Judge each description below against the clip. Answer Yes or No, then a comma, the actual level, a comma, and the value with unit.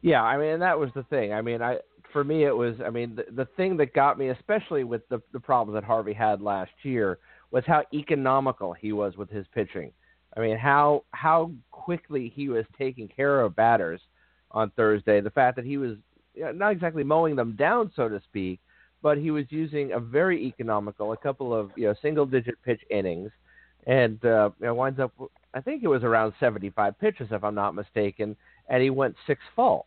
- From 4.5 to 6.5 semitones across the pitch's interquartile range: Yes, average, 5.1 semitones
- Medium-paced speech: No, fast, 220 wpm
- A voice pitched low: Yes, low, 125 Hz